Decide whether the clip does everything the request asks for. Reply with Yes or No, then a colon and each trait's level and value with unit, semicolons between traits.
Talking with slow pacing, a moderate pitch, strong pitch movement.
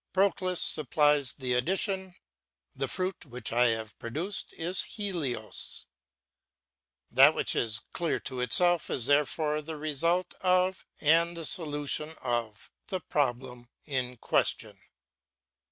Yes: slow, 120 wpm; medium, 150 Hz; wide, 6.0 semitones